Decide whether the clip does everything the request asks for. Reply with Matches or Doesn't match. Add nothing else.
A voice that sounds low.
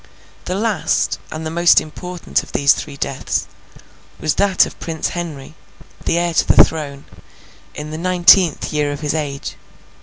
Doesn't match